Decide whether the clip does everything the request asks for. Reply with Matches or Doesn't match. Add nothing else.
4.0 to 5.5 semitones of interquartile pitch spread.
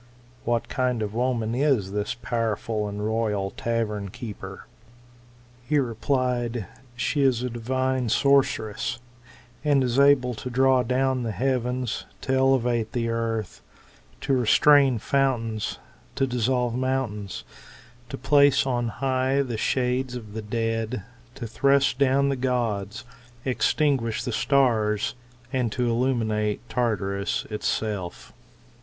Doesn't match